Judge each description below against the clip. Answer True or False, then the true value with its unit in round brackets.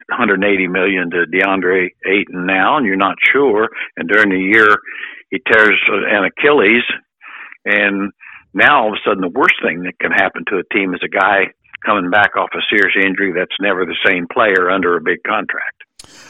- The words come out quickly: False (190 wpm)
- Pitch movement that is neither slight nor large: False (1.2 semitones)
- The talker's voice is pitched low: True (95 Hz)